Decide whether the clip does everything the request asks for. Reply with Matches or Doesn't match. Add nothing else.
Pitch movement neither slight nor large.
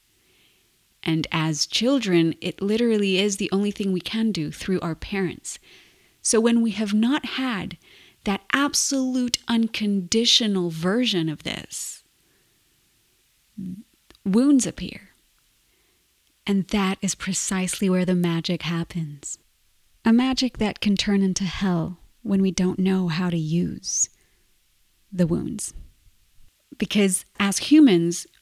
Matches